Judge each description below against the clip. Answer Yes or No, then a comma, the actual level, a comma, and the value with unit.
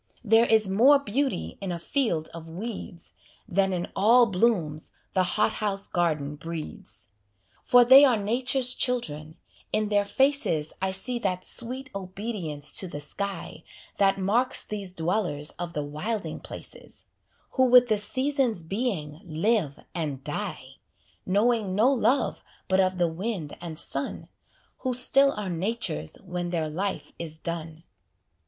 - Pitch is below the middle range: No, high, 195 Hz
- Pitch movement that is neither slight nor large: No, wide, 6.1 semitones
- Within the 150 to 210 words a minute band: No, average, 140 wpm